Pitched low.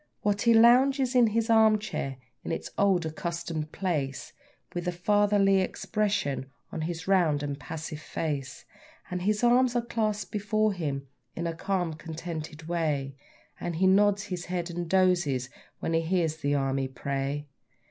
No: medium, 175 Hz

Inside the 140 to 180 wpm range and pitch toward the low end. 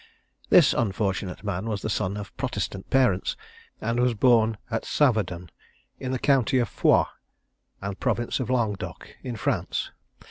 Yes: average, 145 wpm; low, 110 Hz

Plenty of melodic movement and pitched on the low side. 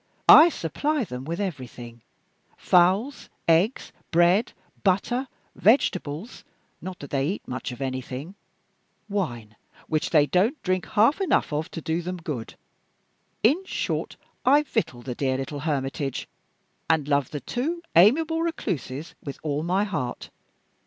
No: wide, 7.5 semitones; medium, 170 Hz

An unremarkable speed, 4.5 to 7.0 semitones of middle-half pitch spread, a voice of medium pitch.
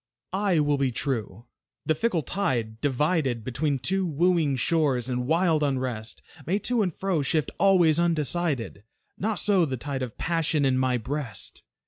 Yes: average, 155 wpm; average, 5.0 semitones; medium, 150 Hz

